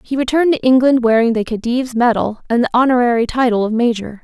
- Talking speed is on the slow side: No, average, 200 wpm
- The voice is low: No, high, 240 Hz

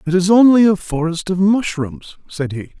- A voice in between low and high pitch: Yes, medium, 180 Hz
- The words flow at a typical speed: Yes, average, 195 wpm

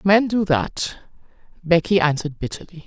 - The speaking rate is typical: No, slow, 125 wpm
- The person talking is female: Yes, female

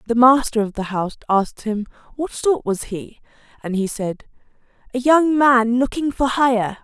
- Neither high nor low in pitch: No, high, 240 Hz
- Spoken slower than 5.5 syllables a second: Yes, 4.7 syllables/s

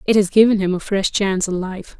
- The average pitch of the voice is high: Yes, high, 195 Hz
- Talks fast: Yes, fast, 270 wpm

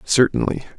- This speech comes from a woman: No, male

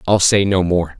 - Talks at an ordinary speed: No, fast, 240 wpm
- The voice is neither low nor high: No, very low, 90 Hz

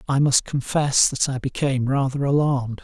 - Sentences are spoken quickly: No, average, 170 wpm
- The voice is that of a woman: No, male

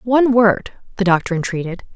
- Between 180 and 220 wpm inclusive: No, average, 155 wpm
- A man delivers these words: No, female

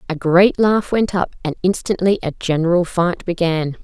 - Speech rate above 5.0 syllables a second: No, 4.8 syllables/s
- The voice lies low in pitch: No, medium, 180 Hz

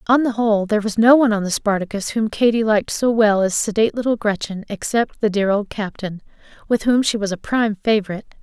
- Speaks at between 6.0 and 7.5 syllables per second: Yes, 6.3 syllables/s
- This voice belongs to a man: No, female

